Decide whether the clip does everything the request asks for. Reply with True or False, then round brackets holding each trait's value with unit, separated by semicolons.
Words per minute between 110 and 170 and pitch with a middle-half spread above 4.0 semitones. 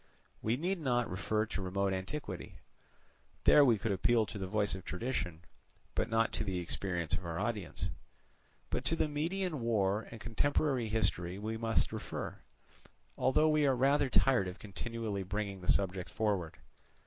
True (160 wpm; 4.9 semitones)